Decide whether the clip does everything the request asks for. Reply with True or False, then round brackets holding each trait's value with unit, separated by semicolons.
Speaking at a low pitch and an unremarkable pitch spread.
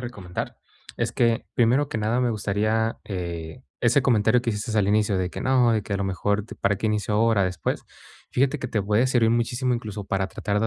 True (110 Hz; 3.0 semitones)